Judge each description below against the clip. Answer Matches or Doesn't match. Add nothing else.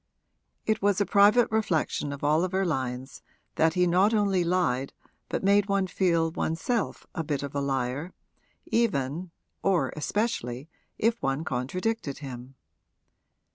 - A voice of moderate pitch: Matches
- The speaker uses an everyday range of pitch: Doesn't match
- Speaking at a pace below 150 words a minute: Matches